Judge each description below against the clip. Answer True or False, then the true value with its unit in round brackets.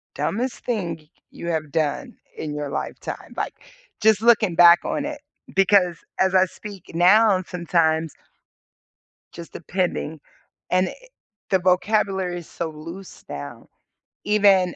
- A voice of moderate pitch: True (180 Hz)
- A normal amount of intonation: True (3.4 semitones)